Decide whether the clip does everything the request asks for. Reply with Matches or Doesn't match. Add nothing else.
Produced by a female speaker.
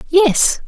Matches